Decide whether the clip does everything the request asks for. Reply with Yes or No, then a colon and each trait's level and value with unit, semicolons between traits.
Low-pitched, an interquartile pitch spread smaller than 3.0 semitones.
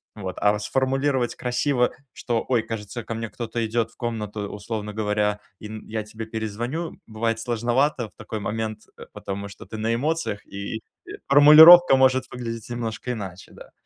Yes: low, 115 Hz; narrow, 2.6 semitones